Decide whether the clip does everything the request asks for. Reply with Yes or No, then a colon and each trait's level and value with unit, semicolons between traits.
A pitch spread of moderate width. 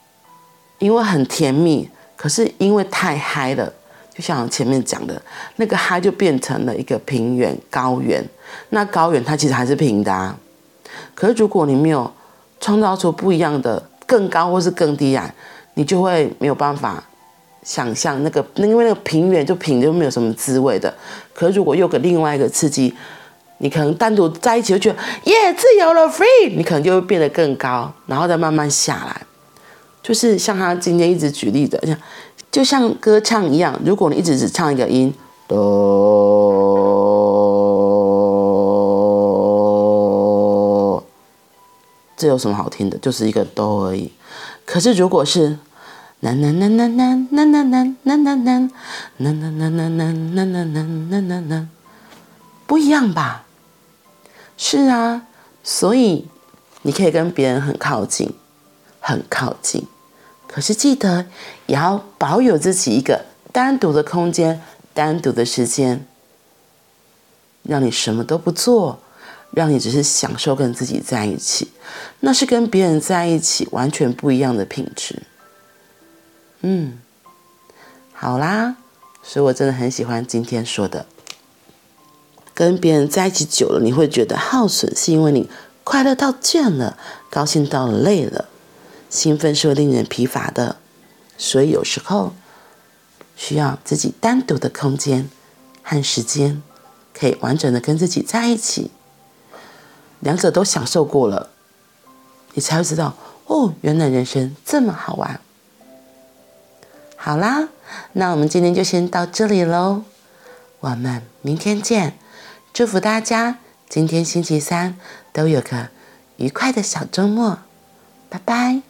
No: wide, 7.4 semitones